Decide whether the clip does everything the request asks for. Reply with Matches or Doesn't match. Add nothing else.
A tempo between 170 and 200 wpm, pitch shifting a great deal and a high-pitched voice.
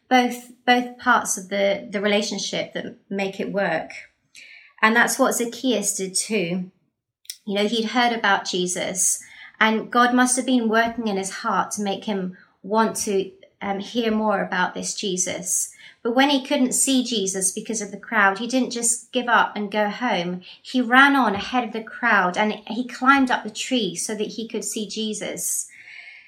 Doesn't match